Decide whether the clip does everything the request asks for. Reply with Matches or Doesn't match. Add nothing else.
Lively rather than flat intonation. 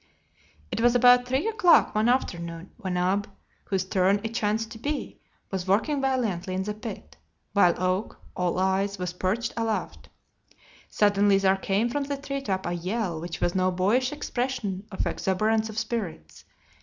Doesn't match